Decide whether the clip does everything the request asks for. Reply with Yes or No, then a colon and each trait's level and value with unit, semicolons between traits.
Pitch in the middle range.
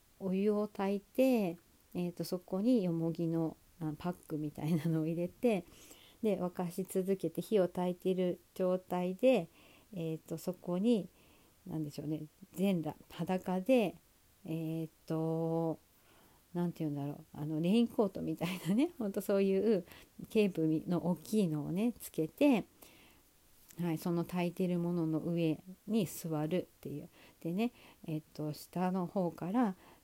Yes: medium, 175 Hz